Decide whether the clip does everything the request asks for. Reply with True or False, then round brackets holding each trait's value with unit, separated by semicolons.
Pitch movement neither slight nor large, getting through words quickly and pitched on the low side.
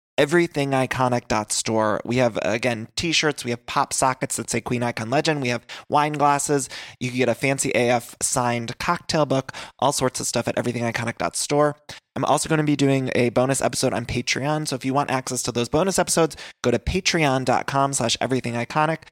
False (3.4 semitones; 175 wpm; 130 Hz)